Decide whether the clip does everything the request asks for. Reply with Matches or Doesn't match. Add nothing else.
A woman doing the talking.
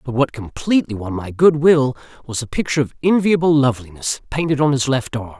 Doesn't match